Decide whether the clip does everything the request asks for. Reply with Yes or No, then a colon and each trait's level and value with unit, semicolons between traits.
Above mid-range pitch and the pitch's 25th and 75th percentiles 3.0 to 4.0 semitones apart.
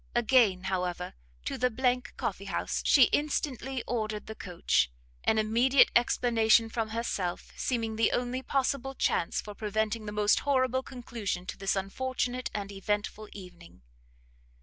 Yes: high, 225 Hz; average, 3.7 semitones